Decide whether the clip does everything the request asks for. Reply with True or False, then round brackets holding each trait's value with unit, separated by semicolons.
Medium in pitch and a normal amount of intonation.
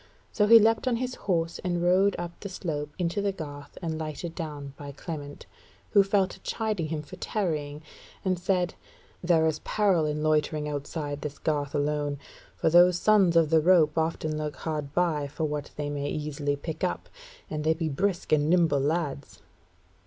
True (160 Hz; 3.3 semitones)